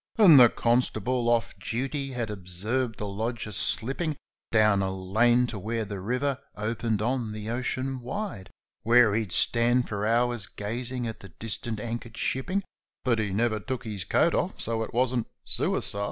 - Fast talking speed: No, average, 165 wpm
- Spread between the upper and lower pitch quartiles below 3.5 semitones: Yes, average, 2.9 semitones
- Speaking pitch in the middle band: No, low, 115 Hz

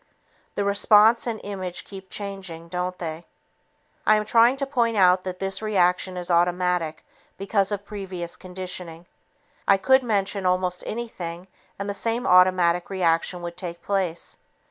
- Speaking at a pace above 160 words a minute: No, average, 145 wpm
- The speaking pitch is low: No, medium, 185 Hz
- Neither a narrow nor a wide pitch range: No, narrow, 2.3 semitones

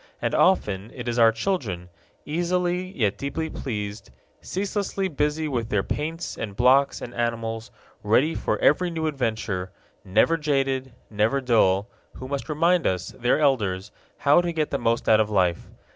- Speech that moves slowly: No, average, 160 wpm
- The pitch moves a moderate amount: No, wide, 6.6 semitones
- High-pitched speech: No, low, 130 Hz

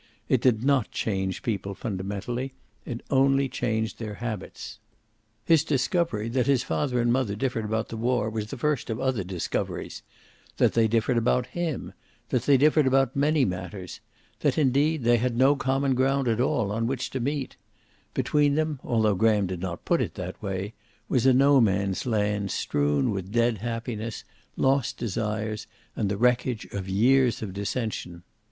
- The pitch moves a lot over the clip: No, average, 4.2 semitones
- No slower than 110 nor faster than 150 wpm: No, average, 170 wpm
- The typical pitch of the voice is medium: No, low, 120 Hz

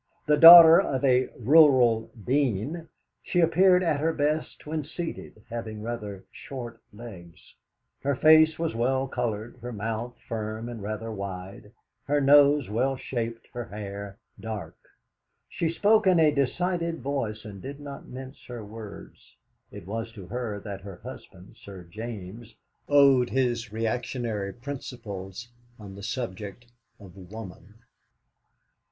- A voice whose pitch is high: No, low, 120 Hz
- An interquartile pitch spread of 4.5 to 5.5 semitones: Yes, average, 5.1 semitones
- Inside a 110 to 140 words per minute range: Yes, slow, 135 wpm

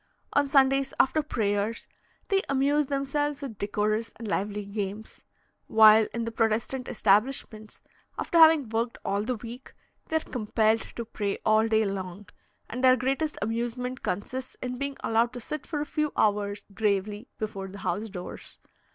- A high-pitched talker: Yes, high, 225 Hz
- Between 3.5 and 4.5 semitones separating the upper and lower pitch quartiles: Yes, average, 4.2 semitones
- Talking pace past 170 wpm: No, average, 160 wpm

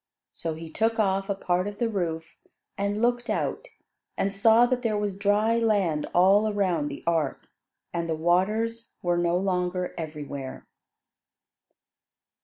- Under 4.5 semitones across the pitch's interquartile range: Yes, average, 4.1 semitones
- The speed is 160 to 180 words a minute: No, average, 145 wpm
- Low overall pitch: No, high, 195 Hz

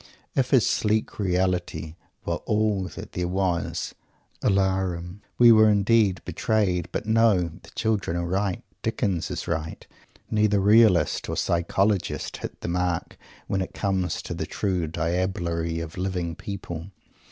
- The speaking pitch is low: Yes, very low, 95 Hz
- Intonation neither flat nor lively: Yes, average, 3.1 semitones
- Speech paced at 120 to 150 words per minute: Yes, average, 140 wpm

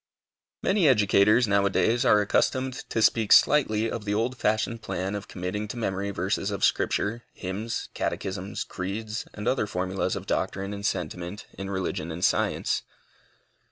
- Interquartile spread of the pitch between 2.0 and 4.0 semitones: Yes, average, 2.7 semitones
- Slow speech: No, average, 155 wpm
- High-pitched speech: No, low, 105 Hz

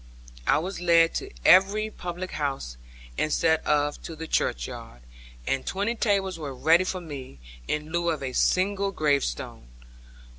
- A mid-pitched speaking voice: Yes, medium, 165 Hz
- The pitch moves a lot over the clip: No, average, 4.2 semitones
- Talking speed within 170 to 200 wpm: No, average, 145 wpm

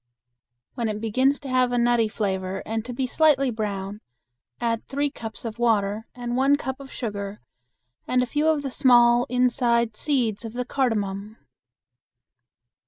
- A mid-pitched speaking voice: No, high, 240 Hz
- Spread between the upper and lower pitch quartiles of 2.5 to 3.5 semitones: Yes, average, 3.0 semitones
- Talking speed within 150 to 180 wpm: Yes, average, 160 wpm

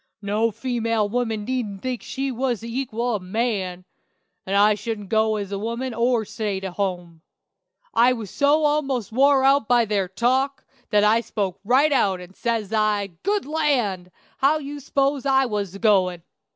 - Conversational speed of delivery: Yes, average, 180 wpm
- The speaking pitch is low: No, high, 225 Hz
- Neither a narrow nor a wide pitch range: Yes, average, 4.4 semitones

